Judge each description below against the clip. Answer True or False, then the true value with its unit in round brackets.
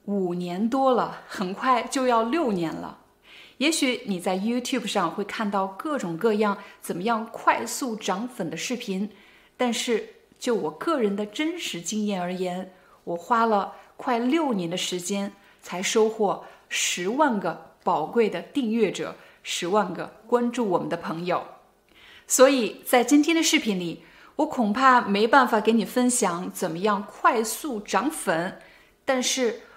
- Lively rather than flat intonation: False (4.5 semitones)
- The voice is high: True (220 Hz)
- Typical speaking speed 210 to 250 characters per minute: True (225 characters per minute)